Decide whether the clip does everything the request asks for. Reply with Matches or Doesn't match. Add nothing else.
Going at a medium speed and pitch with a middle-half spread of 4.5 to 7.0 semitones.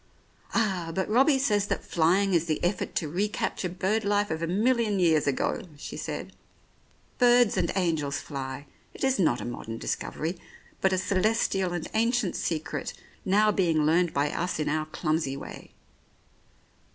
Matches